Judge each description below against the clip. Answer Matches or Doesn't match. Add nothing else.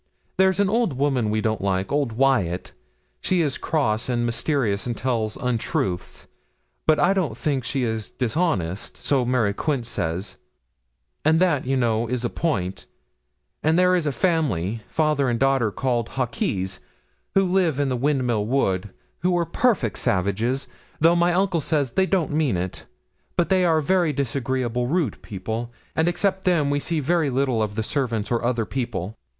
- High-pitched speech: Doesn't match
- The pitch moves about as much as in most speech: Doesn't match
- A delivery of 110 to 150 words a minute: Doesn't match